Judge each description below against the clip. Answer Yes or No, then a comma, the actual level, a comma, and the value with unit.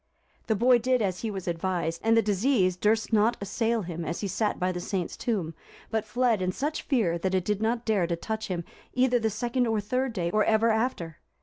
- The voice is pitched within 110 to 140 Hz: No, high, 215 Hz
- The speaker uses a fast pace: Yes, fast, 225 wpm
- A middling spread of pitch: Yes, average, 4.1 semitones